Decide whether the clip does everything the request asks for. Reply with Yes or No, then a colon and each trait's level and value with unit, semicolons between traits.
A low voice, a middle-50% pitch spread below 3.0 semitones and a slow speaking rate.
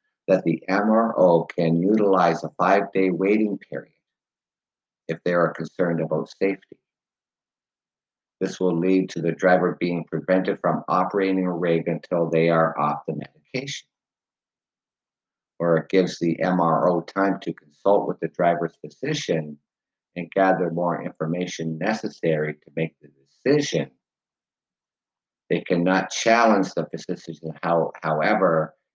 Yes: very low, 85 Hz; narrow, 2.5 semitones; slow, 125 wpm